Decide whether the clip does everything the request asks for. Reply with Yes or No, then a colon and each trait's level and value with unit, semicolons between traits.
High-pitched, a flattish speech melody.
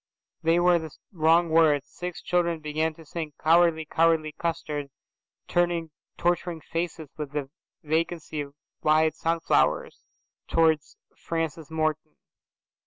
No: medium, 160 Hz; narrow, 1.5 semitones